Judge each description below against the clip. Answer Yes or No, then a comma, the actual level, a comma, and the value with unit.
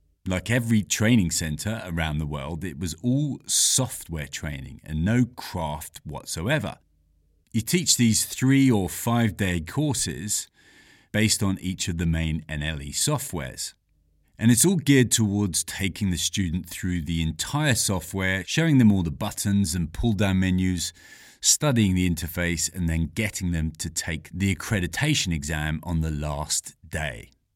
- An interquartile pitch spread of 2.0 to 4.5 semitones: No, wide, 5.4 semitones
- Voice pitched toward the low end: Yes, very low, 90 Hz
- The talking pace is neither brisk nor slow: Yes, average, 150 wpm